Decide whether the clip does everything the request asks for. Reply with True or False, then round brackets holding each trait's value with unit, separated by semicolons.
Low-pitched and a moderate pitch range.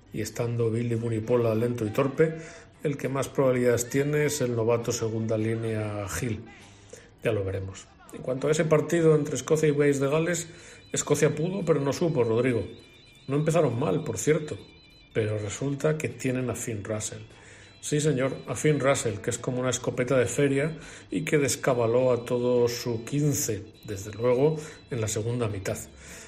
True (125 Hz; 4.7 semitones)